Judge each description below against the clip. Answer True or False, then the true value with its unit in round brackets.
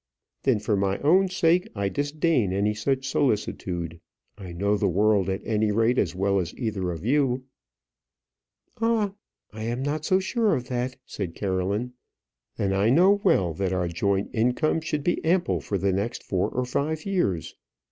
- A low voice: True (110 Hz)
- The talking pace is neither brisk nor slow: True (170 wpm)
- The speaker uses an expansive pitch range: True (6.9 semitones)